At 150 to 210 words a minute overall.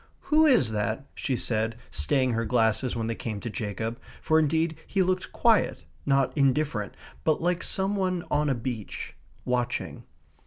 Yes: average, 160 wpm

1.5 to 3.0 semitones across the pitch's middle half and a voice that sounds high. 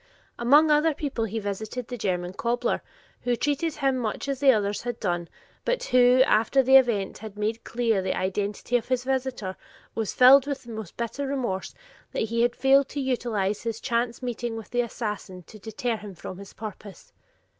No: average, 3.7 semitones; high, 235 Hz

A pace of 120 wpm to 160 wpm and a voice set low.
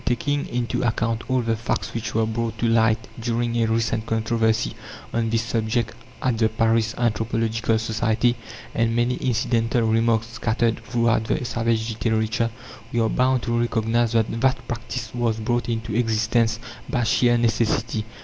Yes: average, 155 wpm; low, 115 Hz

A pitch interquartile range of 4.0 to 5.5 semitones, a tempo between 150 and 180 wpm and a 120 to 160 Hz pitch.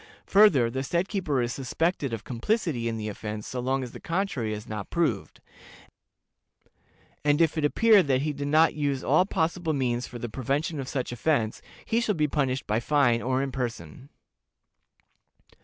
Yes: average, 5.0 semitones; average, 175 wpm; low, 135 Hz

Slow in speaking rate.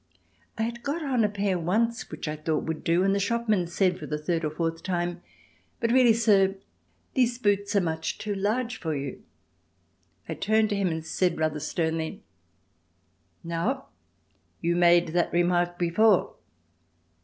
No: average, 165 wpm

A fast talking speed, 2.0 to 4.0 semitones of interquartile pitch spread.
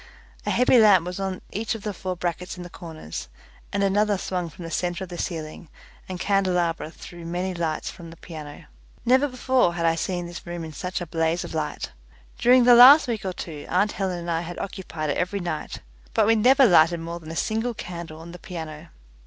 Yes: fast, 220 wpm; average, 3.2 semitones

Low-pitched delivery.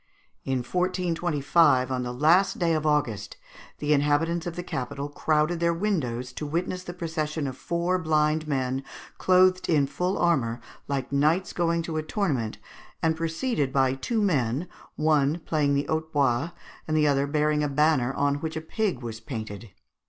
No: medium, 150 Hz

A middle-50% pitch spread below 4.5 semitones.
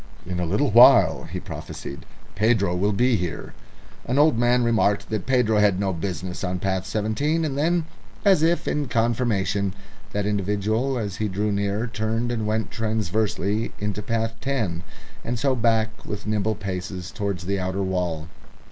Yes: average, 3.3 semitones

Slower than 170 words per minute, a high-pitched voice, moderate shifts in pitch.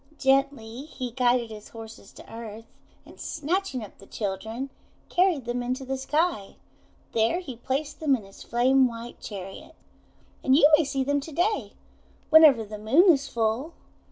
Yes: average, 160 wpm; very high, 260 Hz; average, 4.3 semitones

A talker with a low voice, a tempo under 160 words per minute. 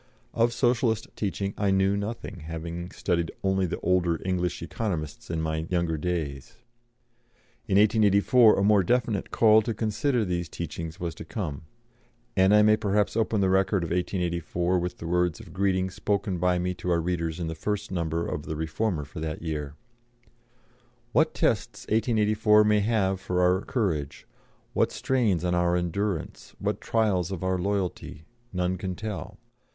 No: very low, 95 Hz; average, 165 wpm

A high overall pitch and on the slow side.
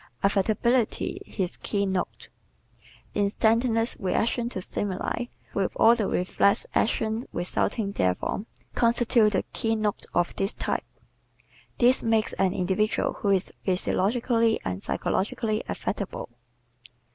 Yes: high, 215 Hz; slow, 110 wpm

